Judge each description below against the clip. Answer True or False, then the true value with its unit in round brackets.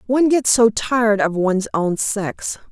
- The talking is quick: False (175 wpm)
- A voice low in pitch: False (220 Hz)